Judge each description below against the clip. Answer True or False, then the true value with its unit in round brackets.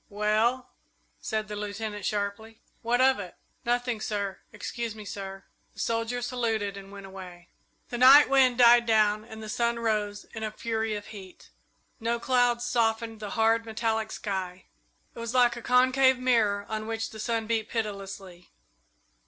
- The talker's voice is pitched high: True (220 Hz)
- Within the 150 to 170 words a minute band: True (160 wpm)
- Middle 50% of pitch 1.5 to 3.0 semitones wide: True (2.4 semitones)